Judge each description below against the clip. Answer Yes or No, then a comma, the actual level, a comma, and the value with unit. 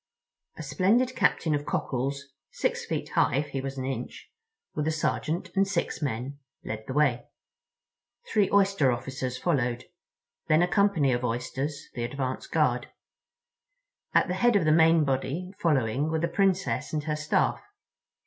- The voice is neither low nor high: Yes, medium, 150 Hz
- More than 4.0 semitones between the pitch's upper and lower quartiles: Yes, average, 5.0 semitones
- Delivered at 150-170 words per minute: Yes, average, 160 wpm